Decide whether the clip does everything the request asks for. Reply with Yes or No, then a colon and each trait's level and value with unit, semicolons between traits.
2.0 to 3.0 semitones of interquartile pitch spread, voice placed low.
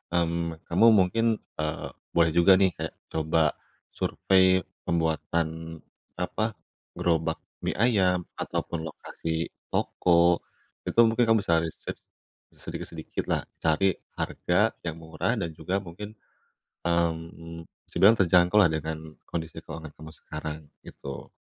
Yes: narrow, 2.5 semitones; very low, 85 Hz